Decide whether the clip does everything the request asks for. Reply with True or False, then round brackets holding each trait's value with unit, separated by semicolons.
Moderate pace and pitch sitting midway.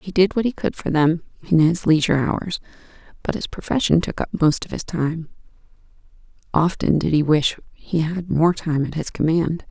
True (190 wpm; 165 Hz)